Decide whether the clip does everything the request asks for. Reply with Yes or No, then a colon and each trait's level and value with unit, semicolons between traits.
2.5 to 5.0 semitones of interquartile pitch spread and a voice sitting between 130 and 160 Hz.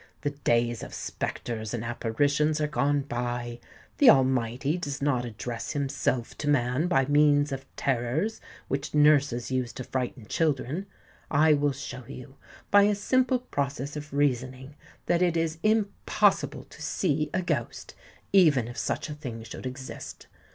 Yes: average, 3.5 semitones; medium, 140 Hz